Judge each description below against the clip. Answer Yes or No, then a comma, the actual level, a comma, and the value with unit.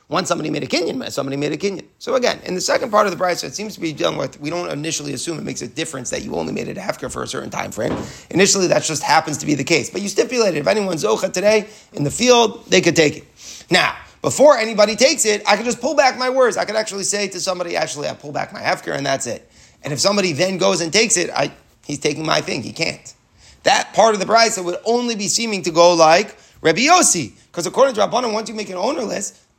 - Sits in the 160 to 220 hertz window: Yes, high, 190 Hz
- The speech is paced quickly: Yes, fast, 265 wpm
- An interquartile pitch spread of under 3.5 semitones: No, average, 5.1 semitones